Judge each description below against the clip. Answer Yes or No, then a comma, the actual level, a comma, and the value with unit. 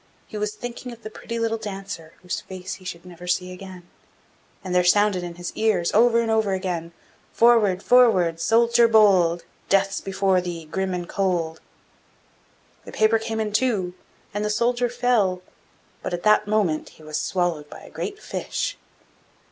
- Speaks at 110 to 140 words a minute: No, average, 170 wpm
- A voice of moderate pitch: No, high, 195 Hz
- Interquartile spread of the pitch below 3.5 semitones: No, average, 3.8 semitones